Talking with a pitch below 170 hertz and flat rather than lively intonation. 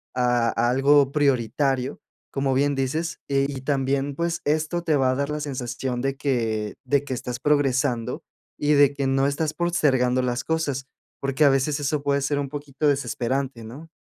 Yes: medium, 140 Hz; narrow, 2.2 semitones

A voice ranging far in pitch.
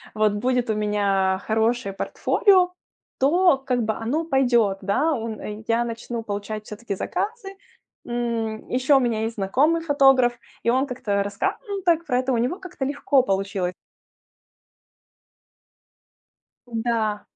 No: average, 4.2 semitones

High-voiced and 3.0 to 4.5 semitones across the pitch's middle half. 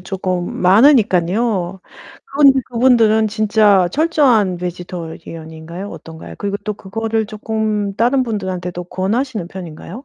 Yes: high, 205 Hz; average, 3.9 semitones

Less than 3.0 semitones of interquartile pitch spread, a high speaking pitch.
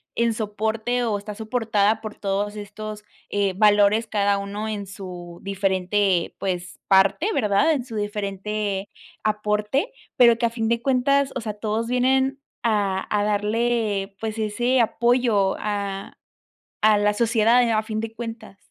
Yes: narrow, 2.4 semitones; high, 215 Hz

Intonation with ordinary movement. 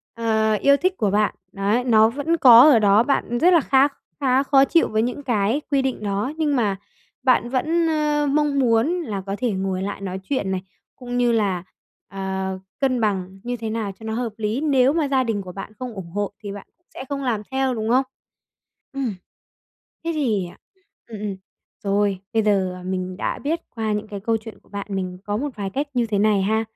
Yes: average, 5.0 semitones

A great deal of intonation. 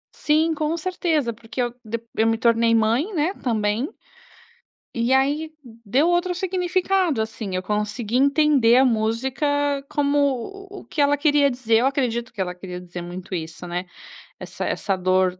Yes: wide, 5.7 semitones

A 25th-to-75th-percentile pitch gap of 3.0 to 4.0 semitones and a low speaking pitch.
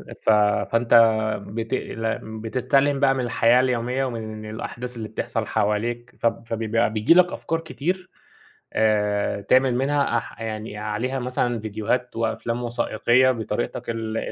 No: narrow, 2.6 semitones; low, 115 Hz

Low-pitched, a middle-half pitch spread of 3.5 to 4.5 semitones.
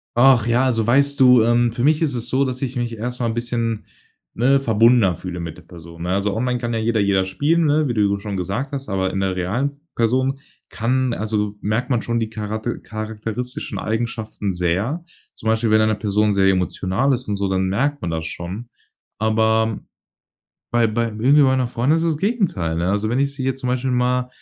Yes: low, 115 Hz; average, 3.8 semitones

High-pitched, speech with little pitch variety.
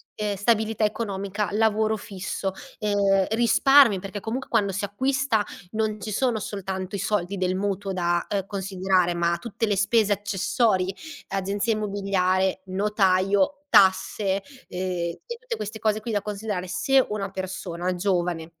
Yes: high, 200 Hz; narrow, 2.3 semitones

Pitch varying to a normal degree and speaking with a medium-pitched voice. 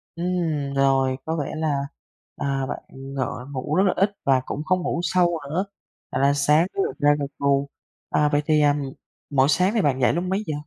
Yes: average, 3.8 semitones; medium, 145 Hz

